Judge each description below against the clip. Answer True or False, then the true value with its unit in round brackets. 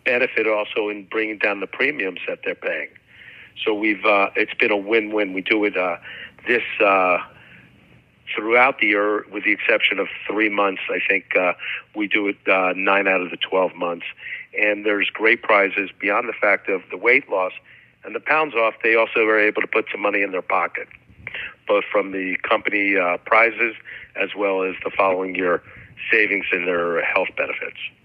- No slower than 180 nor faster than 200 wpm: True (190 wpm)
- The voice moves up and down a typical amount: True (3.0 semitones)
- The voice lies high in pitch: False (105 Hz)